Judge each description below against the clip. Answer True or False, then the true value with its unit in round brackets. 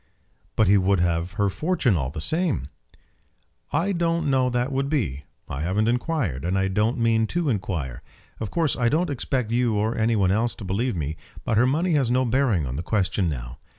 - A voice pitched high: False (110 Hz)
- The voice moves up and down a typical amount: False (6.5 semitones)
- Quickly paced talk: True (210 wpm)